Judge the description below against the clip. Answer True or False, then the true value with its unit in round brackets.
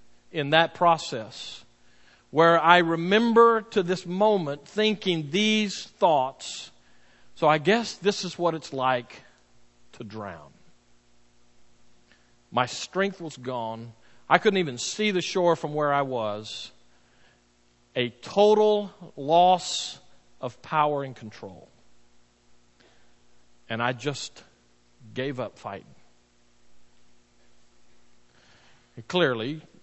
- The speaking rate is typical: False (105 wpm)